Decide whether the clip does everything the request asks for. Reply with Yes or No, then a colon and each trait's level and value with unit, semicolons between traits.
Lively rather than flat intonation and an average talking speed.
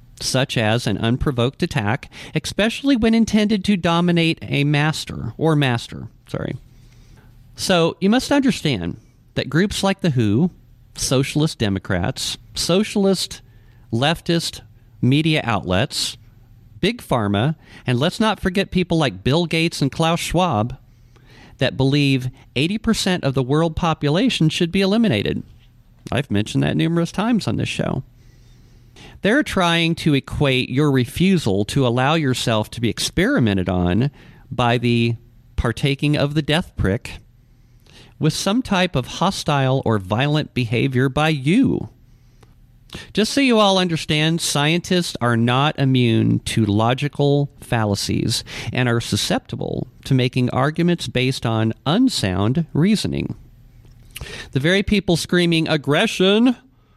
No: wide, 6.1 semitones; slow, 125 wpm